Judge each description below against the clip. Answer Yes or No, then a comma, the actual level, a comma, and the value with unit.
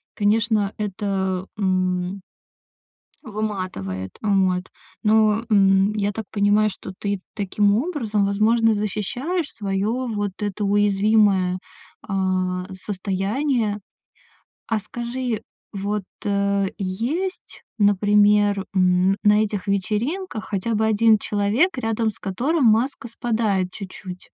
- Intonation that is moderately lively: No, narrow, 2.2 semitones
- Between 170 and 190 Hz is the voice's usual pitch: No, high, 205 Hz